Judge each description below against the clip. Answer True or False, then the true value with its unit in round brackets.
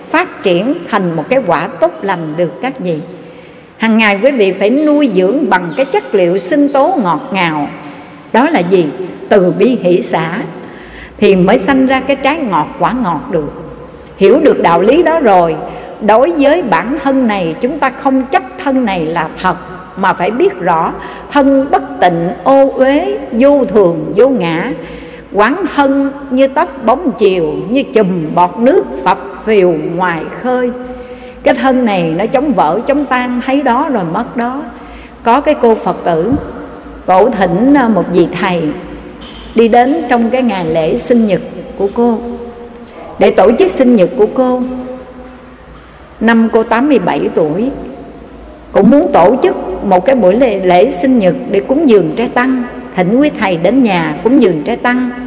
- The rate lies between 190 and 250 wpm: False (170 wpm)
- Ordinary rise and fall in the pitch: False (6.2 semitones)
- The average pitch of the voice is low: False (240 Hz)